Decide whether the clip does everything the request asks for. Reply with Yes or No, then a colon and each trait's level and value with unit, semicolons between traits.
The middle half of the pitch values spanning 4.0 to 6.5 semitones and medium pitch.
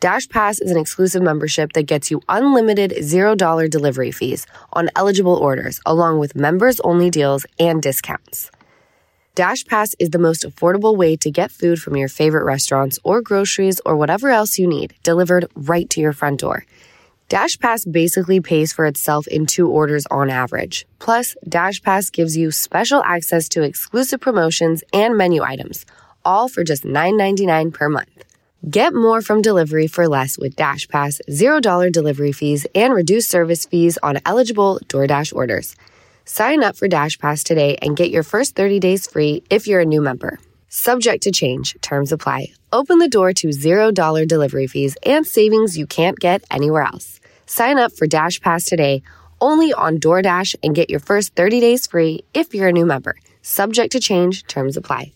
Yes: average, 4.7 semitones; medium, 170 Hz